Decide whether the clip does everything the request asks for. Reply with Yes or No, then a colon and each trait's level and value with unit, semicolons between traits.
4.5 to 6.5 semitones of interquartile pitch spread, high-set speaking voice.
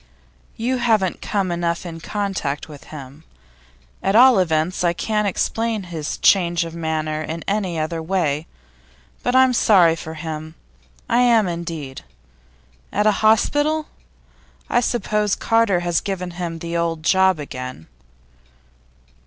No: average, 4.8 semitones; medium, 175 Hz